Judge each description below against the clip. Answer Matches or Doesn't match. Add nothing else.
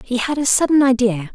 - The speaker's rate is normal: Doesn't match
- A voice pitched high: Matches